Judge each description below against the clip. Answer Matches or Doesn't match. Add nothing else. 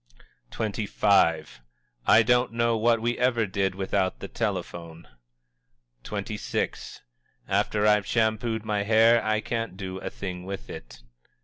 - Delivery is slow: Matches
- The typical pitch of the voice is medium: Doesn't match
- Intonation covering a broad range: Doesn't match